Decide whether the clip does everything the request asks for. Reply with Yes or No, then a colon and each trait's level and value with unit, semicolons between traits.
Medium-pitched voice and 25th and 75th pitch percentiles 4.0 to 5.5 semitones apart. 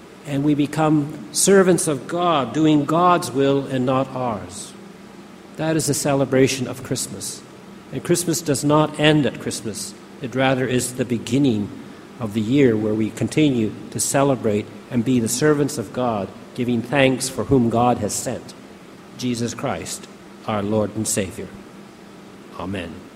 No: low, 130 Hz; average, 4.4 semitones